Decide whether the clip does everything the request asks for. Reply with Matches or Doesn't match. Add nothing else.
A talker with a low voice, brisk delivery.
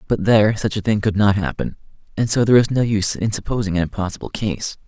Matches